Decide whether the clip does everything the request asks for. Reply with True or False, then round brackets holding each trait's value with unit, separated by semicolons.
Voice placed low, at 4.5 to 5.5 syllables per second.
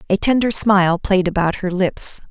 False (190 Hz; 4.9 syllables/s)